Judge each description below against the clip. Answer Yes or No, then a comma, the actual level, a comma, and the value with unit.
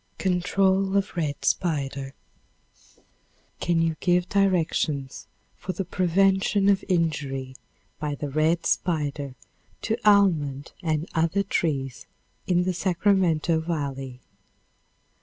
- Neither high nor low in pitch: Yes, medium, 165 Hz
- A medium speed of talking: No, slow, 100 wpm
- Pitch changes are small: No, average, 4.6 semitones